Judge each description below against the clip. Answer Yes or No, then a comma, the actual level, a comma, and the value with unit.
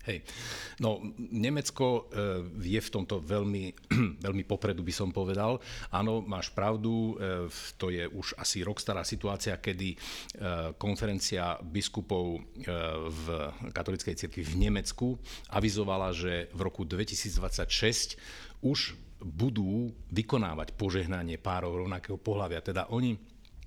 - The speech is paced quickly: No, slow, 110 wpm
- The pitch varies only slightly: No, average, 3.5 semitones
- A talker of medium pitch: No, low, 100 Hz